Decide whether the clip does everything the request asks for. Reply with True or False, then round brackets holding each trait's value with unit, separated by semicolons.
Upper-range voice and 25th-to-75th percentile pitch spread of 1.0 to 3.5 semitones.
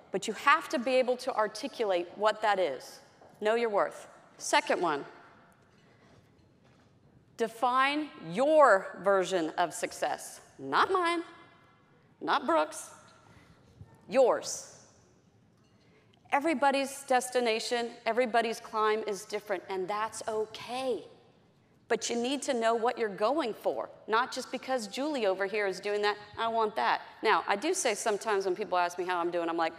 False (225 Hz; 4.4 semitones)